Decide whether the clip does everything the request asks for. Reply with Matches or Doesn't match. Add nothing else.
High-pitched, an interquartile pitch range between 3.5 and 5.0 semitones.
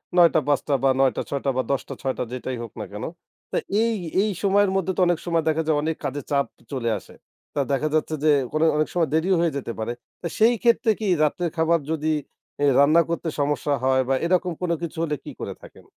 Doesn't match